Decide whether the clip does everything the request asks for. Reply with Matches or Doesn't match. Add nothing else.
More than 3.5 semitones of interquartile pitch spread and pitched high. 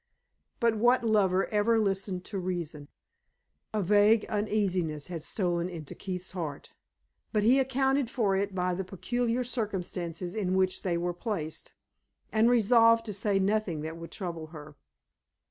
Matches